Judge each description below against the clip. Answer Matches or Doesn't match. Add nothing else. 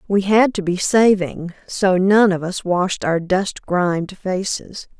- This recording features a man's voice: Doesn't match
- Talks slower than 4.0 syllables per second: Matches